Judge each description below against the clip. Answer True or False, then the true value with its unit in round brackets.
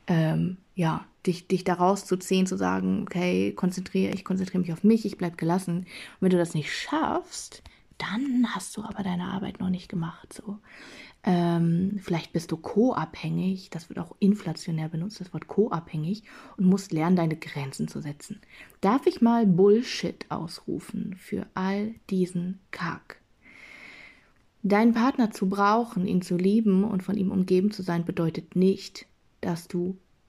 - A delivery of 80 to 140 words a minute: False (160 wpm)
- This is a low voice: False (185 Hz)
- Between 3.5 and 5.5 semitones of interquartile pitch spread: False (2.9 semitones)